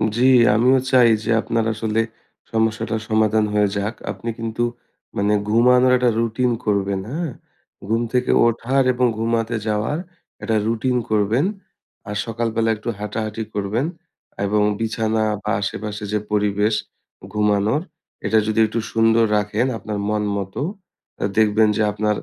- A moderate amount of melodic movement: No, narrow, 1.8 semitones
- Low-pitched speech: Yes, low, 110 Hz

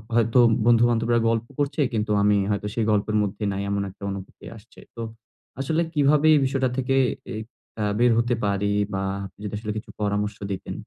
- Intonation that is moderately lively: Yes, average, 3.2 semitones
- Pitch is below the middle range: Yes, low, 110 Hz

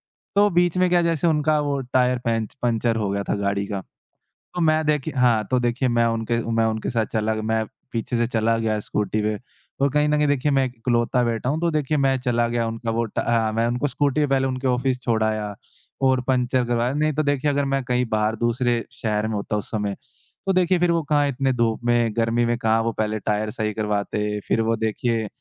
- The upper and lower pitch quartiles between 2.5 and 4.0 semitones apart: Yes, average, 3.7 semitones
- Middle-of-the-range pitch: No, low, 120 Hz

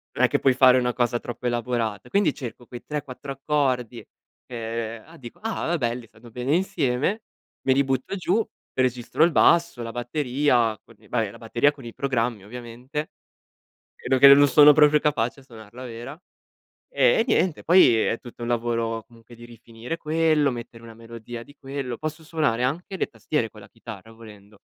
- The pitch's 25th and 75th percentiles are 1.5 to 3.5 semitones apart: No, average, 4.2 semitones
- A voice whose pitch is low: Yes, low, 125 Hz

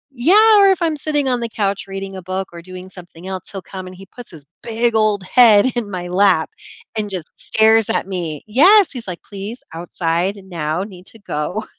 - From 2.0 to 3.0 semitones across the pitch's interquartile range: No, average, 4.2 semitones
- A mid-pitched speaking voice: No, high, 195 Hz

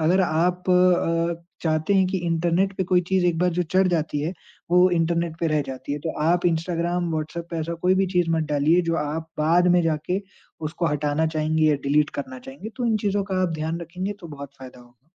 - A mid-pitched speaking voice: Yes, medium, 165 Hz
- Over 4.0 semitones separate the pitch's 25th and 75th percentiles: No, narrow, 2.5 semitones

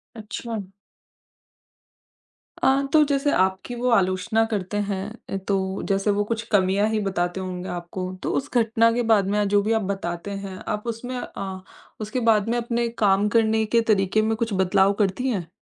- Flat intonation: No, average, 3.1 semitones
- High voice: Yes, high, 205 Hz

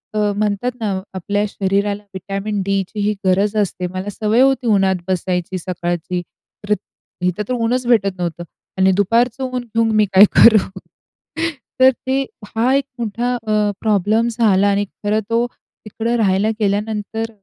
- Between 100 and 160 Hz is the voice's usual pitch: No, high, 210 Hz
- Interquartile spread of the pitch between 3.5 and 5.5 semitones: No, average, 2.8 semitones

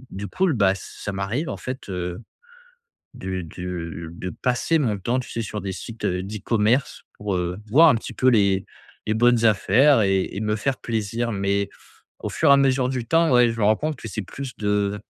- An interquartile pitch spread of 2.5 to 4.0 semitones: No, average, 4.5 semitones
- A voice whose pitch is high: No, low, 110 Hz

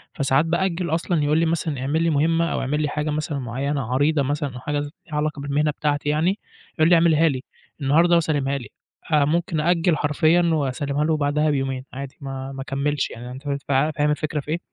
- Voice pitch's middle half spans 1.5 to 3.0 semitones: Yes, narrow, 2.4 semitones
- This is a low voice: No, medium, 150 Hz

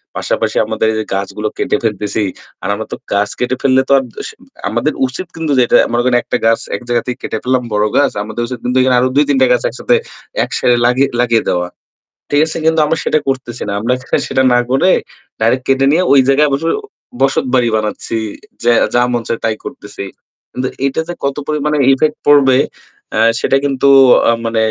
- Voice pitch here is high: No, low, 125 Hz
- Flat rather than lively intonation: No, average, 3.2 semitones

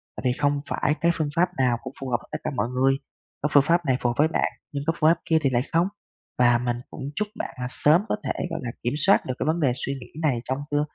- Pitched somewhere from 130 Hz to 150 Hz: Yes, medium, 140 Hz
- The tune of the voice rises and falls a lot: No, average, 4.0 semitones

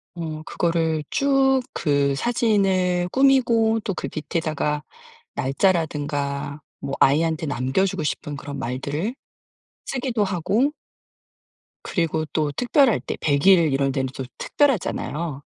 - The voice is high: No, medium, 165 Hz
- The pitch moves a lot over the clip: Yes, wide, 6.9 semitones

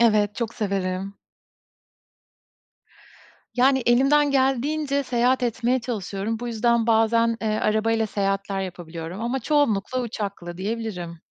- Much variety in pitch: No, average, 3.9 semitones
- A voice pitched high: Yes, high, 225 Hz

